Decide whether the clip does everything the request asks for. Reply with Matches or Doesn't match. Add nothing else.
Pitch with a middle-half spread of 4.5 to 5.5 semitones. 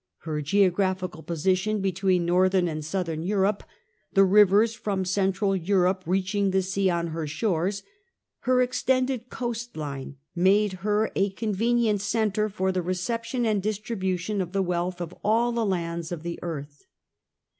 Doesn't match